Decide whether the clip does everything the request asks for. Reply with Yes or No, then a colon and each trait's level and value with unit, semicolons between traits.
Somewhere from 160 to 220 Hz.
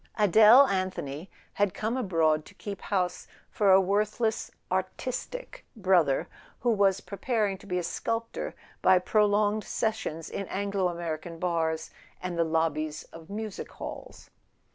Yes: high, 190 Hz